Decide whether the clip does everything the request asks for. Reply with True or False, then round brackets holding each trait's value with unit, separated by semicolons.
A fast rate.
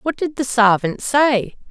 False (175 wpm)